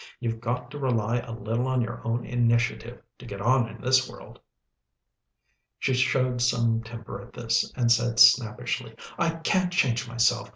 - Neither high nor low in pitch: No, low, 120 Hz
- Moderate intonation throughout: No, narrow, 1.7 semitones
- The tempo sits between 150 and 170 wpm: Yes, average, 165 wpm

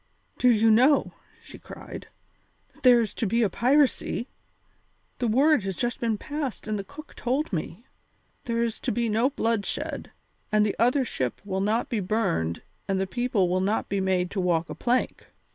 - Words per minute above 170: Yes, average, 185 wpm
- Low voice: No, high, 225 Hz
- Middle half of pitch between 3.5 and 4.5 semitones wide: Yes, average, 4.2 semitones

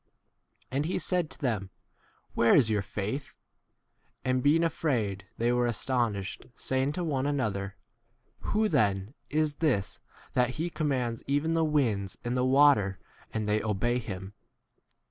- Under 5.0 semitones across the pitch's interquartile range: No, wide, 5.6 semitones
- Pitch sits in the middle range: No, low, 125 Hz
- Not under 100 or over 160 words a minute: Yes, average, 145 wpm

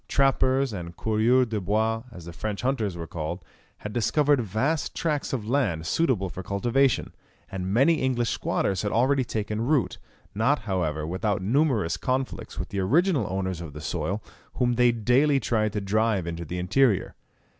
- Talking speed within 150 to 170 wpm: Yes, average, 165 wpm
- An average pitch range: No, wide, 5.7 semitones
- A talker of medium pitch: No, low, 110 Hz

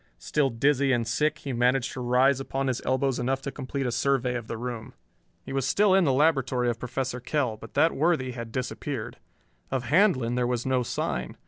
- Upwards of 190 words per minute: Yes, fast, 205 wpm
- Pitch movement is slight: Yes, narrow, 2.2 semitones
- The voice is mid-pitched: No, low, 130 Hz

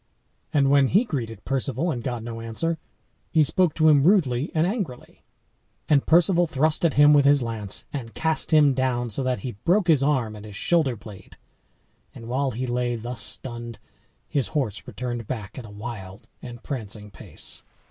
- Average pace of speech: Yes, average, 180 wpm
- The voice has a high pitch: No, low, 130 Hz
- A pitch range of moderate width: Yes, average, 4.6 semitones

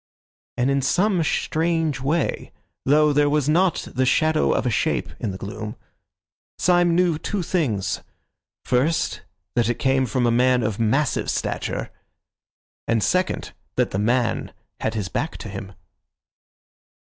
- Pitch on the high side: No, low, 135 Hz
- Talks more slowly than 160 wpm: Yes, average, 145 wpm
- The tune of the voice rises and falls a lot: Yes, wide, 5.7 semitones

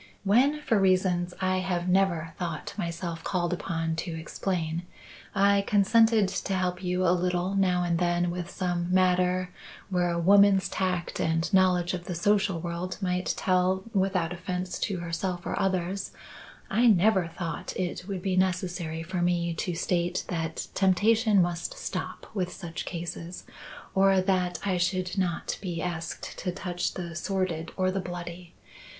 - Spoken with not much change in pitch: Yes, narrow, 1.7 semitones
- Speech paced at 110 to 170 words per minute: Yes, average, 155 wpm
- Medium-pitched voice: Yes, medium, 180 Hz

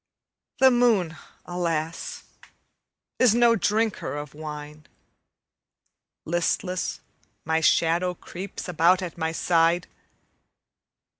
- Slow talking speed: Yes, slow, 85 wpm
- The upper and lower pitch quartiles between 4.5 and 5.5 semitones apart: No, average, 2.9 semitones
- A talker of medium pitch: Yes, medium, 175 Hz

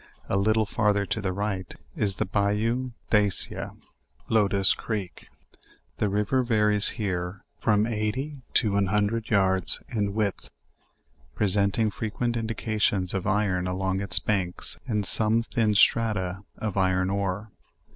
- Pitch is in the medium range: No, low, 105 Hz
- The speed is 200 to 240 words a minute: No, slow, 135 wpm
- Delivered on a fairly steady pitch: Yes, narrow, 2.2 semitones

